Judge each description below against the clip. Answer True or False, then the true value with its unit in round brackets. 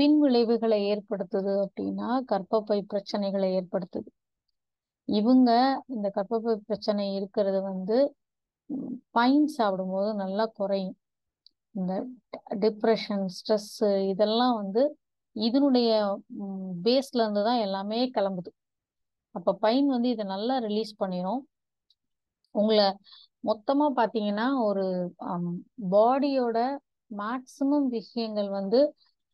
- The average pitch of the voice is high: True (215 Hz)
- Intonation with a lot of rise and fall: False (3.8 semitones)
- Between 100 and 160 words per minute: False (85 wpm)